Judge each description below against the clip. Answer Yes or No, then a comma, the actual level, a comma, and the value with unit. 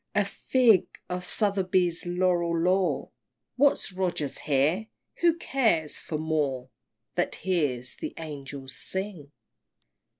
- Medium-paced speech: No, slow, 105 wpm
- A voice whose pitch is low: No, medium, 175 Hz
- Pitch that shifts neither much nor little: Yes, average, 4.5 semitones